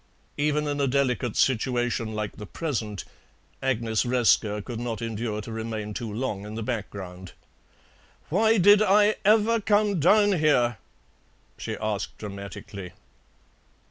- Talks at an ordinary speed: No, slow, 130 wpm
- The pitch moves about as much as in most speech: No, wide, 6.1 semitones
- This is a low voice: Yes, low, 120 Hz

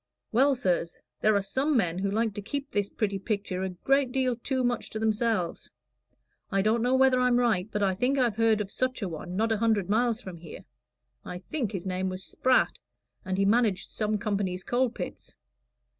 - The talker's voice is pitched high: Yes, high, 215 Hz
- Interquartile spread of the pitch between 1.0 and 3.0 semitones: No, average, 4.2 semitones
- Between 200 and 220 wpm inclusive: Yes, fast, 205 wpm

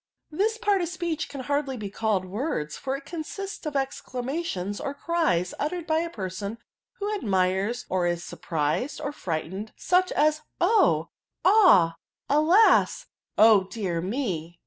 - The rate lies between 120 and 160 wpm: Yes, average, 155 wpm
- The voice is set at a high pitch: Yes, very high, 265 Hz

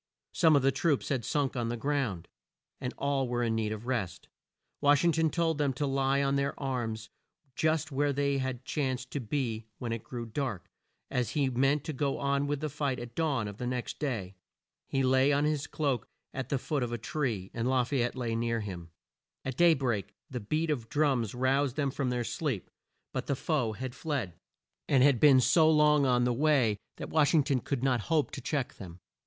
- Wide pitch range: No, average, 3.3 semitones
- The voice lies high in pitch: No, low, 135 Hz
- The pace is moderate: No, fast, 215 wpm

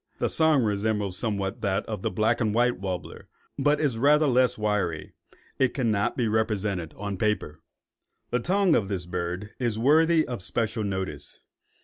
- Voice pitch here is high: No, low, 110 Hz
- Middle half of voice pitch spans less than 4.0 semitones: No, average, 4.3 semitones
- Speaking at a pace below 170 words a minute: Yes, average, 160 wpm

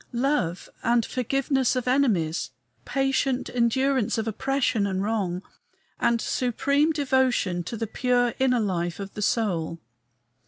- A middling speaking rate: No, slow, 125 wpm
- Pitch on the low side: No, high, 235 Hz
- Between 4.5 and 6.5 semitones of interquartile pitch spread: Yes, average, 4.9 semitones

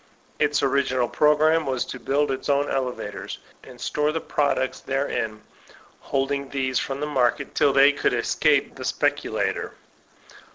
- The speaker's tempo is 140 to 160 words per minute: Yes, average, 150 wpm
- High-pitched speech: No, medium, 140 Hz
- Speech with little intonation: Yes, narrow, 1.9 semitones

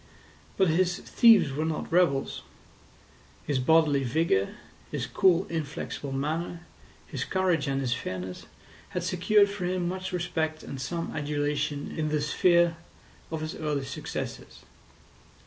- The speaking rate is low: Yes, slow, 130 wpm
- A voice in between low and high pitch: Yes, medium, 160 Hz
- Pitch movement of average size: Yes, average, 3.7 semitones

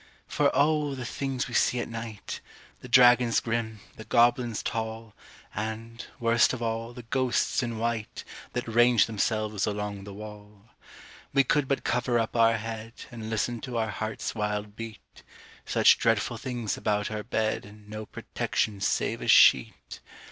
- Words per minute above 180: No, average, 160 wpm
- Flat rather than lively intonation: Yes, narrow, 2.0 semitones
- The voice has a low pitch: Yes, low, 115 Hz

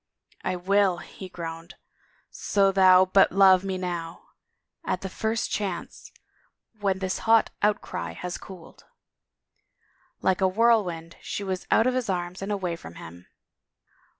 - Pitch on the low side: No, medium, 185 Hz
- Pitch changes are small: Yes, narrow, 2.3 semitones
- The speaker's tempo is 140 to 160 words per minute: Yes, average, 150 wpm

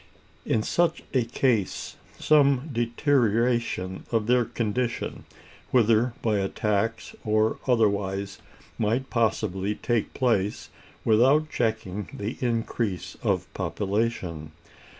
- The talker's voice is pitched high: No, low, 115 Hz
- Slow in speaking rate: Yes, slow, 100 wpm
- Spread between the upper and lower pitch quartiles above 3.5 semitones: No, average, 3.1 semitones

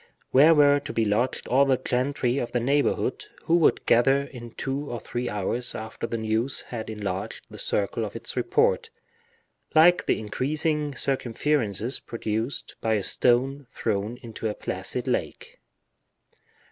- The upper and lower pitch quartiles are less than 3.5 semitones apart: No, average, 4.2 semitones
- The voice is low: Yes, low, 125 Hz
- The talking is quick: No, average, 150 wpm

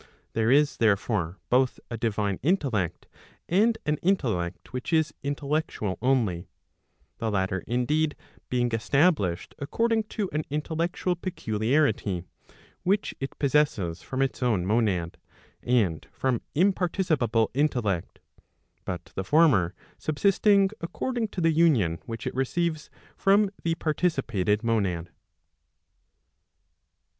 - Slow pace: Yes, slow, 115 wpm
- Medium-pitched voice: No, low, 130 Hz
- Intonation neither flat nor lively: No, wide, 7.9 semitones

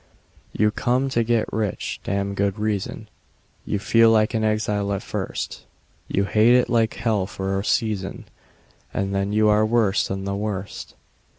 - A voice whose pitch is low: Yes, low, 105 Hz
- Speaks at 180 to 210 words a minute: No, average, 165 wpm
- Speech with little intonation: Yes, narrow, 2.1 semitones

